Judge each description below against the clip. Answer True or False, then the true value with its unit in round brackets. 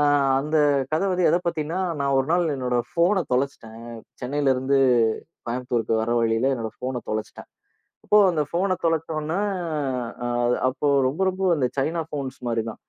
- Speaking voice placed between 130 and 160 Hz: True (140 Hz)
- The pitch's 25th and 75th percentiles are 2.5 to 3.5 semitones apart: False (4.8 semitones)